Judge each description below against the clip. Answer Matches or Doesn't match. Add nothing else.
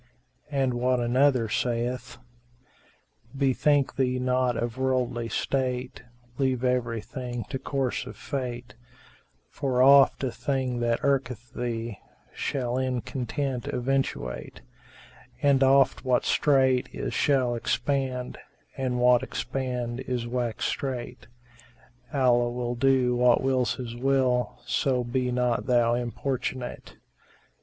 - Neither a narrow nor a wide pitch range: Doesn't match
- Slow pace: Matches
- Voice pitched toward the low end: Matches